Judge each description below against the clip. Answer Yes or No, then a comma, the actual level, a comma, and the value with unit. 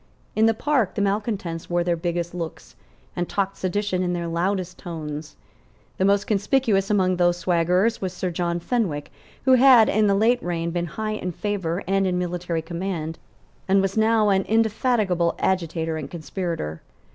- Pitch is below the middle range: No, medium, 185 Hz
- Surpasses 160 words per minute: Yes, average, 170 wpm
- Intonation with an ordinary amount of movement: Yes, average, 3.2 semitones